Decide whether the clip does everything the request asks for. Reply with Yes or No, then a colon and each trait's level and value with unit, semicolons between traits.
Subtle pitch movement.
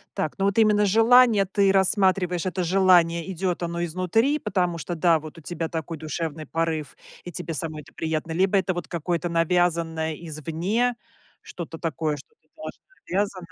No: average, 3.0 semitones